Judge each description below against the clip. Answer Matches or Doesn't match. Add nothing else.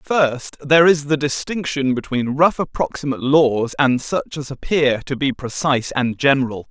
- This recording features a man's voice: Matches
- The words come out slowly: Doesn't match